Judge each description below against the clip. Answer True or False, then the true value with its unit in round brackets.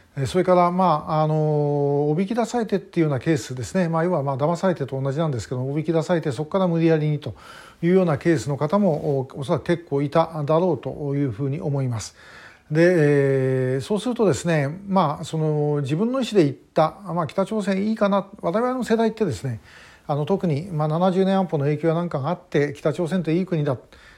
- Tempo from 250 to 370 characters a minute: False (405 characters per minute)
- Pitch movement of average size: True (4.2 semitones)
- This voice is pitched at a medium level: True (160 Hz)